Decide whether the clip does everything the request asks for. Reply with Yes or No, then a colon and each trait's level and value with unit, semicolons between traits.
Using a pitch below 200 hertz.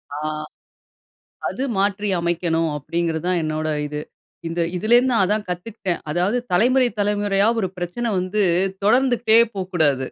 Yes: high, 190 Hz